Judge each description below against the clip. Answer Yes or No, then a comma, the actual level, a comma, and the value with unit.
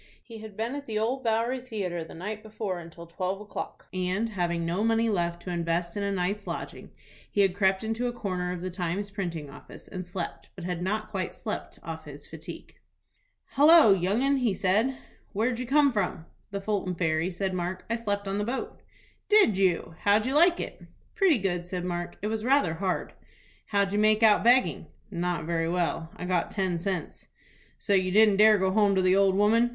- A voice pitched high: Yes, high, 195 Hz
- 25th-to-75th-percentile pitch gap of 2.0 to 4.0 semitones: Yes, average, 3.6 semitones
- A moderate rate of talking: No, fast, 210 wpm